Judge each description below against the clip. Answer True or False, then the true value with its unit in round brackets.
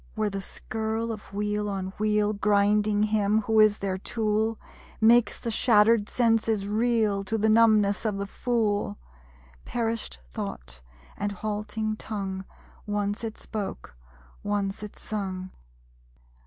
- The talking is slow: True (130 wpm)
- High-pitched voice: True (210 Hz)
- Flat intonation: True (1.5 semitones)